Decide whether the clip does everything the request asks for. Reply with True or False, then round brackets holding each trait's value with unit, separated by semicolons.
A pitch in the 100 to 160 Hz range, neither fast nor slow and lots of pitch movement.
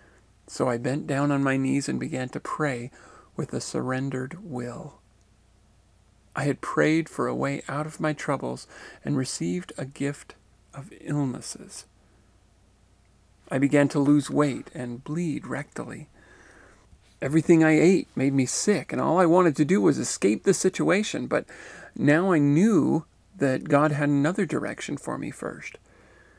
True (140 Hz; 150 wpm; 6.7 semitones)